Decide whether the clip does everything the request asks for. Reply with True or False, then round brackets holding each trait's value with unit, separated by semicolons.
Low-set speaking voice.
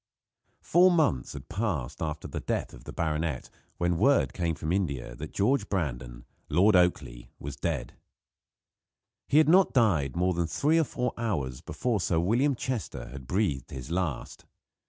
True (85 Hz)